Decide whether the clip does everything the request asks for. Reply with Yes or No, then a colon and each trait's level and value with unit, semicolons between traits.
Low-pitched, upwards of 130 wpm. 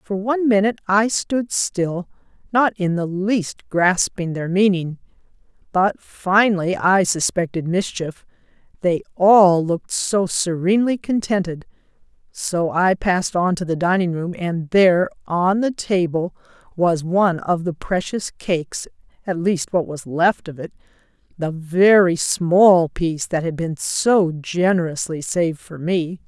No: medium, 180 Hz; average, 140 wpm